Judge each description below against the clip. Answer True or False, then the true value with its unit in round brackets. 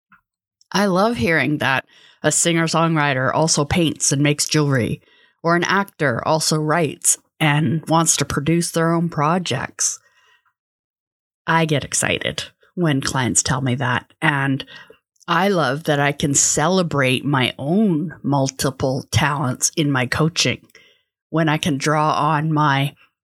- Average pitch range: True (3.1 semitones)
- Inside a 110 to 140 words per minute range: True (135 wpm)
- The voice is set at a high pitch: False (150 Hz)